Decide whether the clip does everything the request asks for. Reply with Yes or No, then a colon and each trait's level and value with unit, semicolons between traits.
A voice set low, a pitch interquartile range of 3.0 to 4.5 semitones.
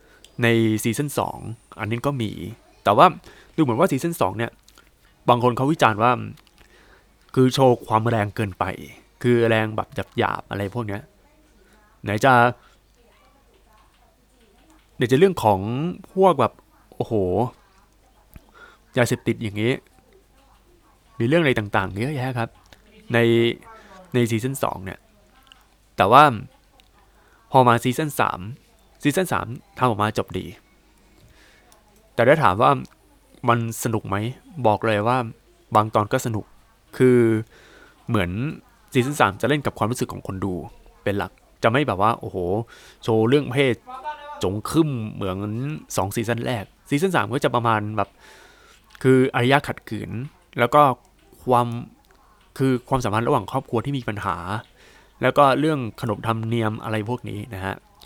Yes: low, 120 Hz; average, 3.3 semitones